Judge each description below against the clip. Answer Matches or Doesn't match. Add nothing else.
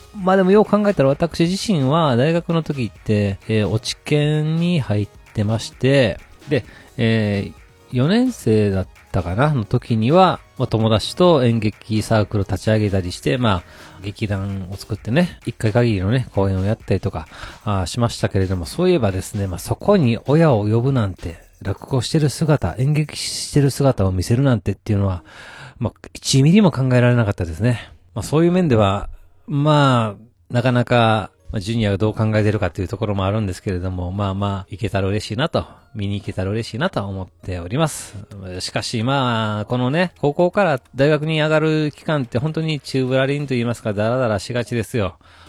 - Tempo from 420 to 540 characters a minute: Doesn't match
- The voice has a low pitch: Matches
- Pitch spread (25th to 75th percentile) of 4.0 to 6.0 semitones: Matches